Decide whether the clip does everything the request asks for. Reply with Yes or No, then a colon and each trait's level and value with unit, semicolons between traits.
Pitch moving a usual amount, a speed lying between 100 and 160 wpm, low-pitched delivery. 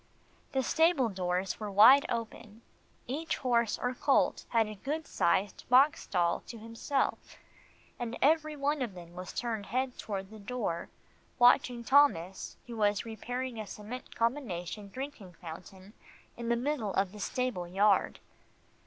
No: average, 4.6 semitones; average, 145 wpm; high, 230 Hz